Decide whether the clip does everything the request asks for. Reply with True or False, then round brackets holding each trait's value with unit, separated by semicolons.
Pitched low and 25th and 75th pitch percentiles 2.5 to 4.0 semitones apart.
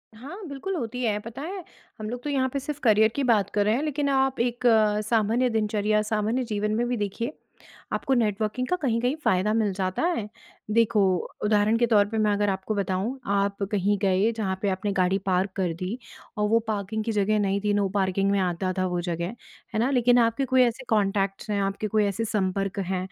False (215 Hz; 3.3 semitones)